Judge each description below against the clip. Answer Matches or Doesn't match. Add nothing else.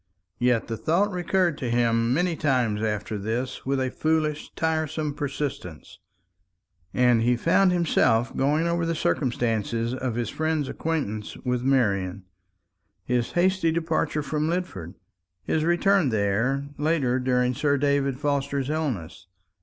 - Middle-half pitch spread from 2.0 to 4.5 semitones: Doesn't match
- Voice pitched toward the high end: Doesn't match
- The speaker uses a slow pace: Matches